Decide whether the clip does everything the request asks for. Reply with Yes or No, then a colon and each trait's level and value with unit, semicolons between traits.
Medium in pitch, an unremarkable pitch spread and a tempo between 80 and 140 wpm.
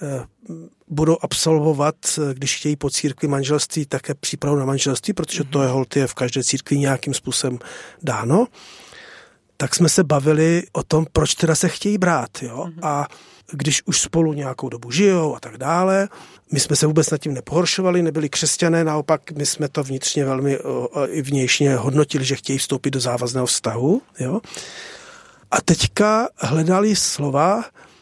No: medium, 150 Hz; average, 3.4 semitones; average, 155 wpm